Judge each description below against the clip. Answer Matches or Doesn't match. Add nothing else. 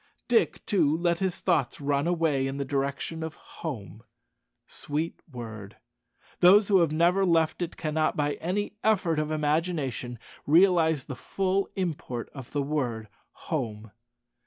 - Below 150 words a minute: Matches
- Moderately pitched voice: Matches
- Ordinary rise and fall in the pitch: Matches